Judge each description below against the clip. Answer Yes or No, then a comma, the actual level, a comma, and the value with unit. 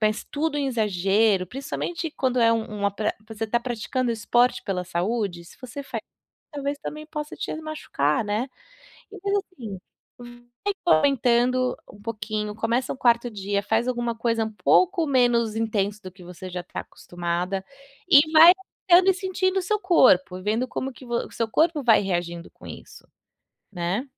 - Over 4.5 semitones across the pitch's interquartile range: Yes, average, 5.1 semitones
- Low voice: No, high, 235 Hz